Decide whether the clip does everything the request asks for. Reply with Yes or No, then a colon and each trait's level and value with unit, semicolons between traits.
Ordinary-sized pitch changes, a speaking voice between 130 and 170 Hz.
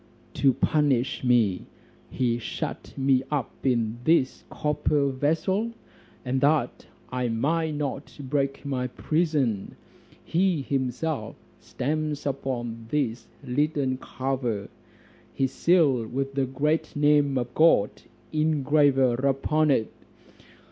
Yes: average, 3.1 semitones; low, 135 Hz